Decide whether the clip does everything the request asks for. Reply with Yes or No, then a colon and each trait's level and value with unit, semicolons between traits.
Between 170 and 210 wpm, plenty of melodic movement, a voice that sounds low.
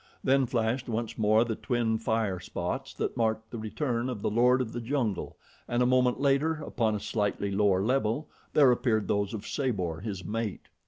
No: average, 190 wpm; average, 3.0 semitones; low, 115 Hz